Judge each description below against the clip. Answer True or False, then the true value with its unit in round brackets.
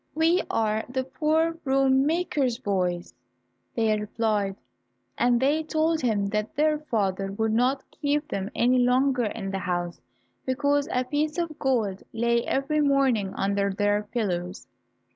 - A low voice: False (245 Hz)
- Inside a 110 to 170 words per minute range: True (145 wpm)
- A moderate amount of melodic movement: False (5.7 semitones)